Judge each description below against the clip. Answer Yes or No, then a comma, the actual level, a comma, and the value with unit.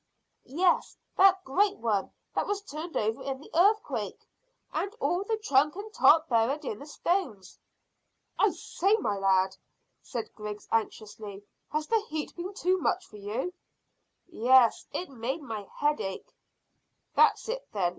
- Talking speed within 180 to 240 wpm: No, average, 155 wpm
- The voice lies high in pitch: Yes, very high, 295 Hz